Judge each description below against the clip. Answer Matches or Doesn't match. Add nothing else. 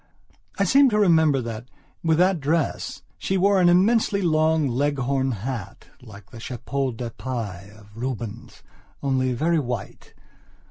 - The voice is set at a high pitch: Doesn't match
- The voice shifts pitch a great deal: Matches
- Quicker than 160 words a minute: Doesn't match